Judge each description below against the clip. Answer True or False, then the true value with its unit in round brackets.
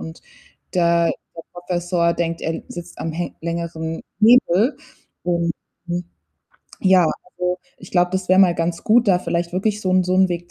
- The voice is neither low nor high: True (175 Hz)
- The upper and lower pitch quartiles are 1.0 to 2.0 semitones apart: True (1.5 semitones)